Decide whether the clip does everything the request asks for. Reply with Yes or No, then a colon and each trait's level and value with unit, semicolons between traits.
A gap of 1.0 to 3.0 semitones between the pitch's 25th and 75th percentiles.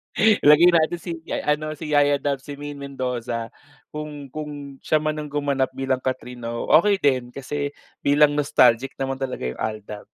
Yes: narrow, 2.5 semitones